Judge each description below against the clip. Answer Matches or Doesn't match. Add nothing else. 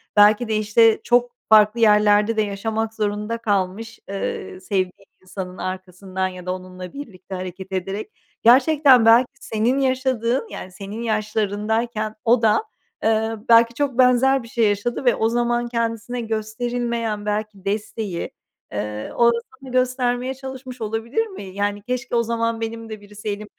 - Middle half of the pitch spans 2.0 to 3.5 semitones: Matches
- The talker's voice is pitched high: Matches